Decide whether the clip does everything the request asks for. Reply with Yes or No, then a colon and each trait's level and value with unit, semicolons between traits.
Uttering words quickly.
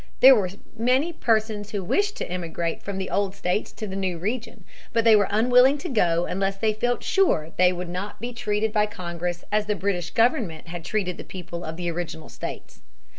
Yes: fast, 210 wpm